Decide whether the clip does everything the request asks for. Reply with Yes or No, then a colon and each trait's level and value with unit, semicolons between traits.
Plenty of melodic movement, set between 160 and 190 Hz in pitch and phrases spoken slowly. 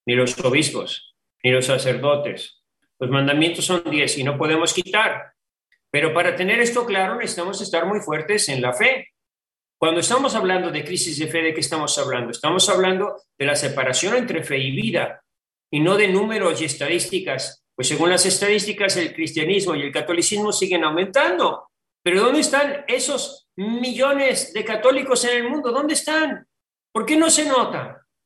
No: wide, 7.1 semitones; medium, 185 Hz; average, 170 wpm